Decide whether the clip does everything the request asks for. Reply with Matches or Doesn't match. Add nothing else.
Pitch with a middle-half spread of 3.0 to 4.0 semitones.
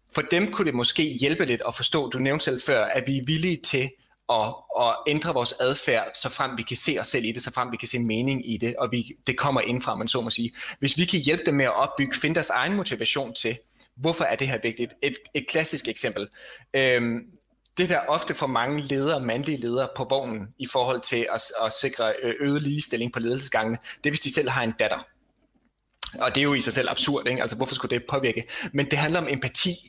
Matches